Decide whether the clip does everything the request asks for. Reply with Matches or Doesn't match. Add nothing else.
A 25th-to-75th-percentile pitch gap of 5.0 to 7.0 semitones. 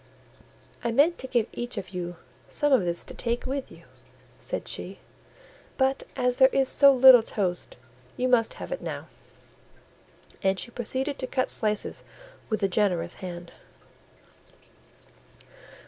Matches